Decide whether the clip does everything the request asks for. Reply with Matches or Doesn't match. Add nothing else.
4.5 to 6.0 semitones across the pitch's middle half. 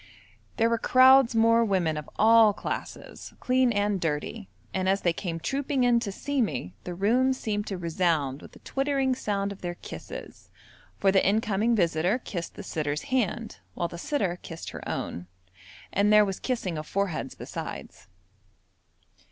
Matches